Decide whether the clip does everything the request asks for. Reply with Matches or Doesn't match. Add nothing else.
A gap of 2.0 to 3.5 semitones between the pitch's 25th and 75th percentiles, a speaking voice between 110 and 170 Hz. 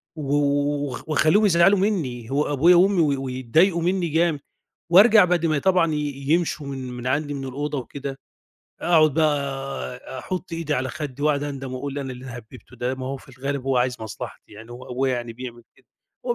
Doesn't match